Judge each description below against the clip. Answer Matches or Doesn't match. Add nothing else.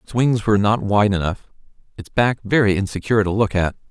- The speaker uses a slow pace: Doesn't match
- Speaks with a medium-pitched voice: Doesn't match